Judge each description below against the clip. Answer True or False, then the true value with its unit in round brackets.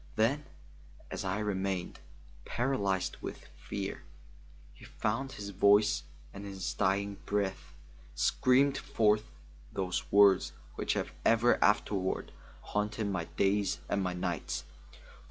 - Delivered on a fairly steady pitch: True (2.1 semitones)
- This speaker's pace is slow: True (120 wpm)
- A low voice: True (100 Hz)